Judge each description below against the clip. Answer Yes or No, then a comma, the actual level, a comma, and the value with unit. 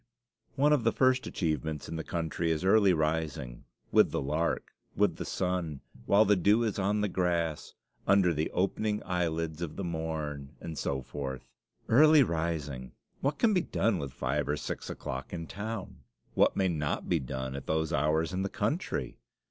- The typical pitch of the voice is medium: No, very low, 85 Hz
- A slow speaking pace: No, average, 180 wpm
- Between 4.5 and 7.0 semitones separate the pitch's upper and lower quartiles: Yes, average, 4.8 semitones